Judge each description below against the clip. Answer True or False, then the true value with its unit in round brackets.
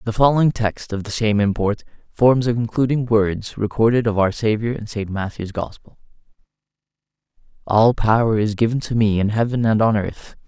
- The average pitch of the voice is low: True (110 Hz)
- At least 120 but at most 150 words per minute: False (170 wpm)